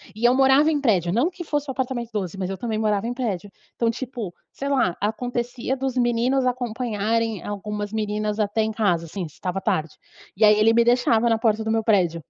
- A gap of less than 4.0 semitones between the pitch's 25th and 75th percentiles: Yes, average, 3.1 semitones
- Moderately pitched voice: No, high, 225 Hz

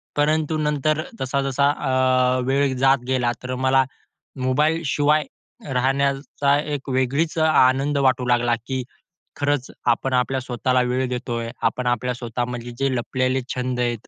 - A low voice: Yes, low, 130 Hz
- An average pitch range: No, narrow, 2.0 semitones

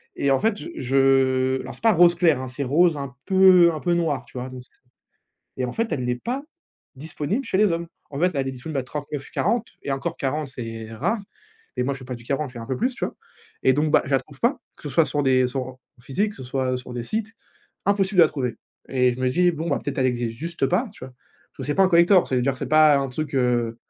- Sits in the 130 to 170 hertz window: Yes, medium, 140 Hz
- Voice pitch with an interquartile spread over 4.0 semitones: Yes, average, 5.0 semitones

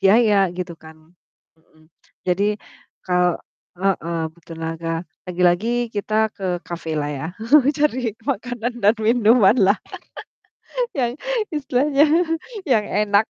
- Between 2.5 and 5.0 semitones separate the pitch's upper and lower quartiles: No, wide, 5.4 semitones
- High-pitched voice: Yes, high, 205 Hz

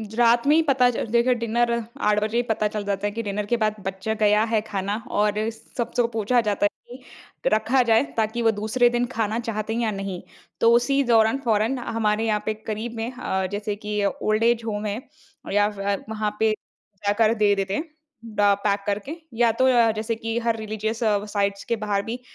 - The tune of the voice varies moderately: No, narrow, 2.2 semitones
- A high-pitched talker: Yes, high, 220 Hz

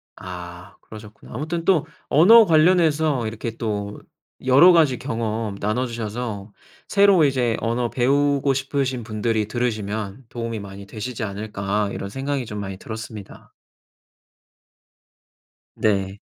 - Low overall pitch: Yes, low, 115 Hz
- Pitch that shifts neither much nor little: Yes, average, 4.7 semitones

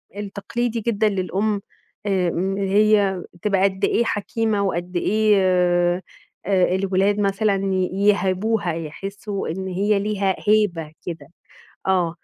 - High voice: Yes, high, 195 Hz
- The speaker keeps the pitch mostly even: Yes, narrow, 2.2 semitones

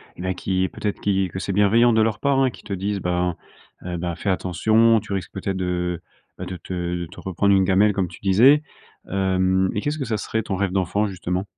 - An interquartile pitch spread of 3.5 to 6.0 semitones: No, narrow, 2.5 semitones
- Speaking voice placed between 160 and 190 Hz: No, very low, 95 Hz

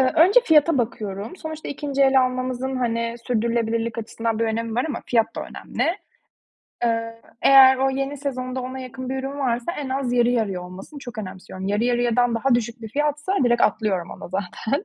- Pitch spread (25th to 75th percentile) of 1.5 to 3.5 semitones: Yes, average, 2.8 semitones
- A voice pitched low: No, high, 245 Hz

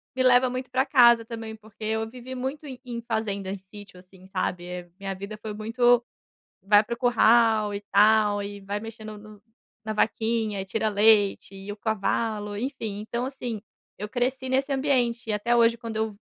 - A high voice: Yes, high, 220 Hz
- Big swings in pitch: No, average, 2.8 semitones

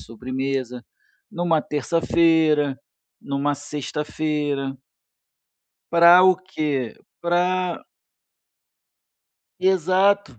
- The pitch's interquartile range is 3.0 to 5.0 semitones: Yes, average, 4.2 semitones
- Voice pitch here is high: No, medium, 155 Hz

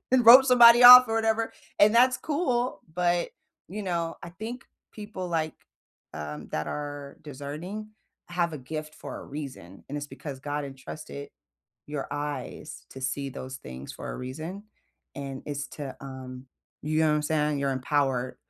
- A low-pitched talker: No, medium, 150 Hz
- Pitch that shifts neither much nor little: No, wide, 6.7 semitones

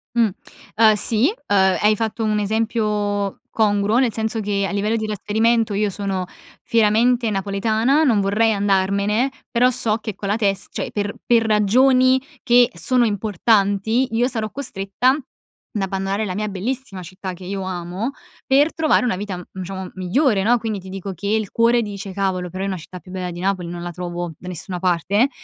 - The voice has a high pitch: Yes, high, 205 Hz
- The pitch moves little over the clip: No, average, 3.0 semitones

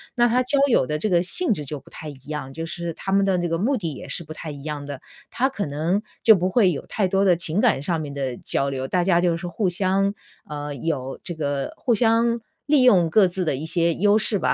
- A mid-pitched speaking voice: Yes, medium, 175 Hz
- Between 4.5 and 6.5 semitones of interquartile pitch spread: Yes, average, 5.1 semitones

